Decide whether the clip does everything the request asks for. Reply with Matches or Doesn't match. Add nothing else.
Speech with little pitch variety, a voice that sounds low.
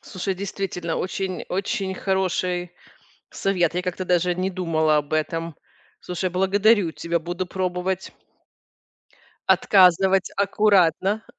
Doesn't match